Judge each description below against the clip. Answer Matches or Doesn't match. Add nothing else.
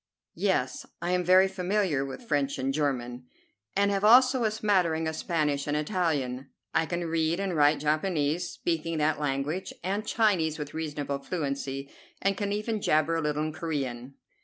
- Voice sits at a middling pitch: Matches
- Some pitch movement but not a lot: Matches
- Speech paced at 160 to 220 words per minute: Matches